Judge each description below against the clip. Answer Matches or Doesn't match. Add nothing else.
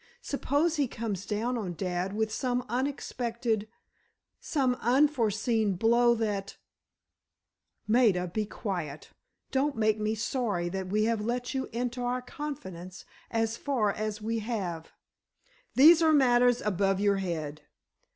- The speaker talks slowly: Matches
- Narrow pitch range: Doesn't match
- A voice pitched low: Doesn't match